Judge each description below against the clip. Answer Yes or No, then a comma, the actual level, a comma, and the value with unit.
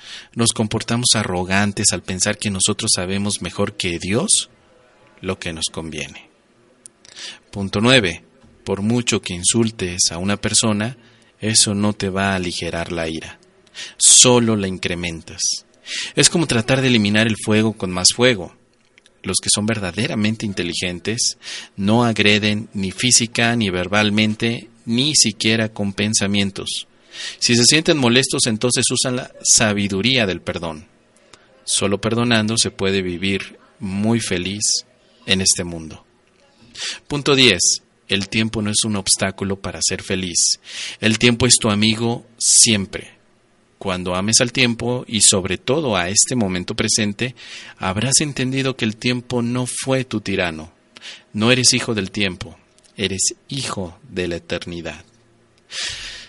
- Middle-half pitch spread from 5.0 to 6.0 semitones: No, average, 3.6 semitones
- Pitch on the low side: Yes, low, 105 Hz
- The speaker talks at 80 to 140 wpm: Yes, average, 135 wpm